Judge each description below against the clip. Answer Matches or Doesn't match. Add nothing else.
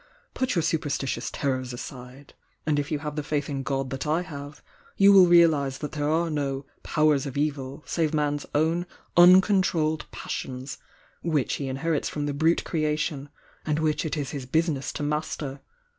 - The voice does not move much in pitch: Matches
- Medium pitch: Matches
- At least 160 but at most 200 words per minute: Matches